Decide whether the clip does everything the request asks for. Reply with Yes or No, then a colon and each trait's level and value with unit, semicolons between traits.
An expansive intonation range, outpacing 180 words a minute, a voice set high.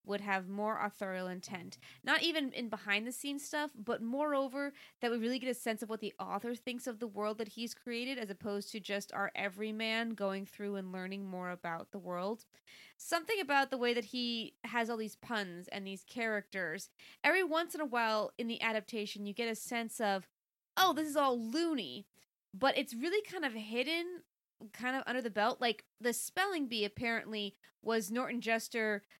No: average, 3.8 semitones; average, 195 wpm; high, 230 Hz